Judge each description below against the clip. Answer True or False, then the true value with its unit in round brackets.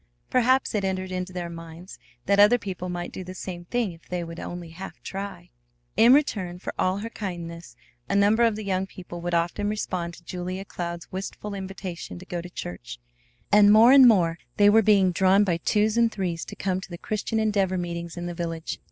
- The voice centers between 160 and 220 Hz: True (185 Hz)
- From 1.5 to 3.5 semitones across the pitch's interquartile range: True (3.0 semitones)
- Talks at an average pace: False (210 wpm)